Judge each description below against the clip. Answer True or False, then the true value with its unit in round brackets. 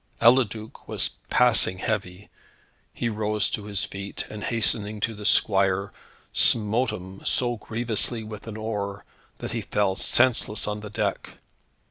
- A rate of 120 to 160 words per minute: True (140 wpm)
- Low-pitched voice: True (105 Hz)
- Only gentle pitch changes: True (2.0 semitones)